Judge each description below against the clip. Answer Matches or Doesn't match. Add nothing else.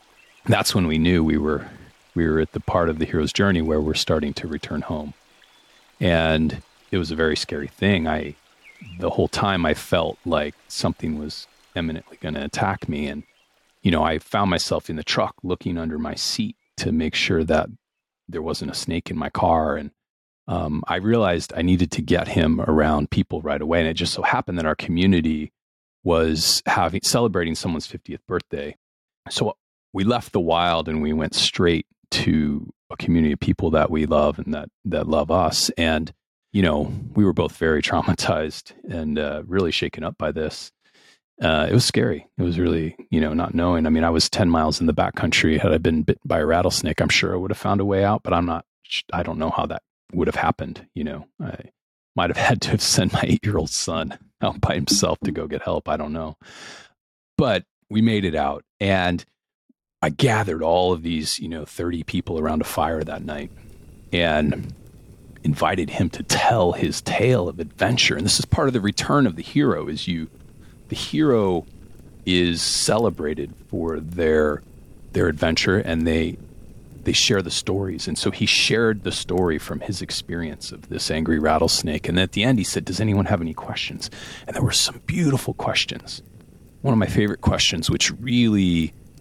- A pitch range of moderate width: Matches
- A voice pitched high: Doesn't match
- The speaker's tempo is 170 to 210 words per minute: Matches